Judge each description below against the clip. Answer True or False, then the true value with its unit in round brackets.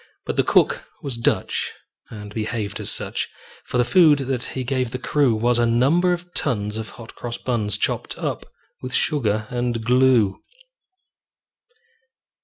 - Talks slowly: False (155 wpm)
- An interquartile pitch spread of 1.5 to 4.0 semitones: True (3.0 semitones)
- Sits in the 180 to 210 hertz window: False (120 Hz)